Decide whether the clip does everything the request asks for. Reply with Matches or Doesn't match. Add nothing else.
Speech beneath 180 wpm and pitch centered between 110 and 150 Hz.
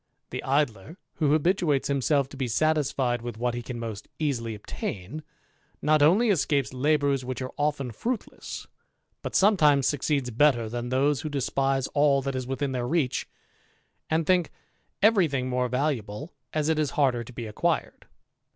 Matches